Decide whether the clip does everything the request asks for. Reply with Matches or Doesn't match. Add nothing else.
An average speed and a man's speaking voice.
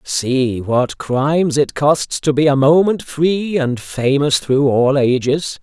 Matches